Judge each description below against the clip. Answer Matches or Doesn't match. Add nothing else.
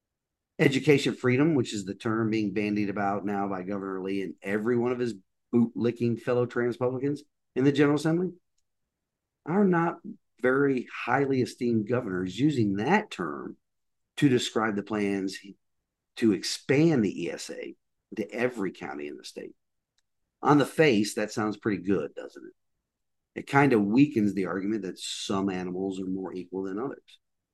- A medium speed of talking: Matches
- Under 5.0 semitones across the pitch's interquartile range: Doesn't match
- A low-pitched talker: Matches